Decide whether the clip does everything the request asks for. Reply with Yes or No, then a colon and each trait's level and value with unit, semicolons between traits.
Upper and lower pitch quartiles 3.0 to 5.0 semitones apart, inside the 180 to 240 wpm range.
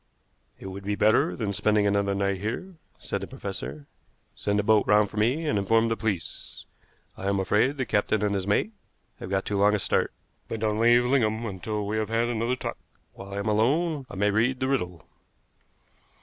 No: narrow, 2.6 semitones; fast, 205 wpm